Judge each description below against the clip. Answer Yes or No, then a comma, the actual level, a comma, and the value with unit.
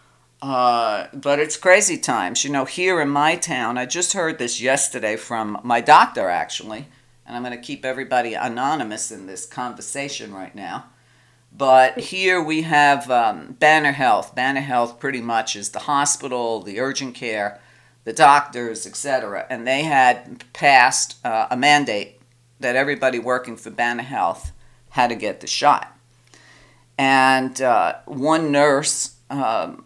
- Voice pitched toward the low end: Yes, low, 130 Hz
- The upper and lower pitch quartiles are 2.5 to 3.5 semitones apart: Yes, average, 2.9 semitones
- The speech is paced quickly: No, average, 150 wpm